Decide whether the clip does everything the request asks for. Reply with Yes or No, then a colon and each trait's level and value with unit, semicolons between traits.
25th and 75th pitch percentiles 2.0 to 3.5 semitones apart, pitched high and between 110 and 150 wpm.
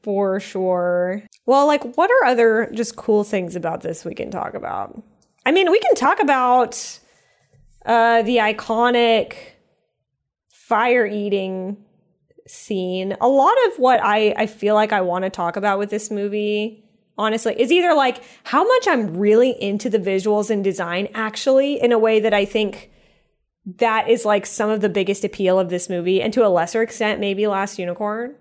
No: average, 3.1 semitones; high, 215 Hz; average, 175 wpm